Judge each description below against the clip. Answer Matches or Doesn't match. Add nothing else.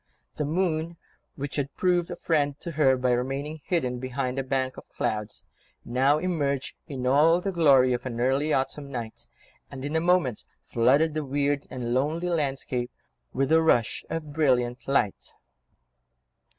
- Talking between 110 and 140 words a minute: Doesn't match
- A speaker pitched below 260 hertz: Matches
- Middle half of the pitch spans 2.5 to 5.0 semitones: Matches